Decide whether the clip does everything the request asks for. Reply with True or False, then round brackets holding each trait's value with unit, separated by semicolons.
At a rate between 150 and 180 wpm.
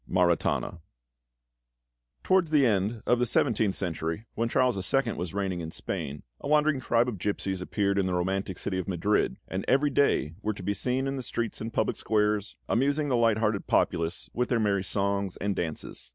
False (190 wpm)